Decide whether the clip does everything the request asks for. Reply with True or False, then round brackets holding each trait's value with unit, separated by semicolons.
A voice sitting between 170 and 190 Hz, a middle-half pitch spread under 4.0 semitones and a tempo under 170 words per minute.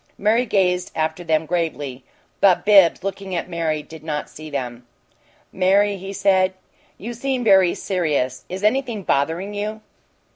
False (185 Hz; 4.4 semitones; 145 wpm)